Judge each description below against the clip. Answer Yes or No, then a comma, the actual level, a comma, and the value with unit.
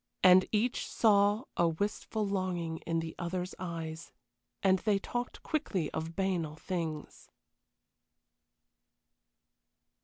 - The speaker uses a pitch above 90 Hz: Yes, medium, 185 Hz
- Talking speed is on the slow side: Yes, slow, 100 wpm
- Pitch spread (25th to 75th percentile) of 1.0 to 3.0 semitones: No, average, 3.6 semitones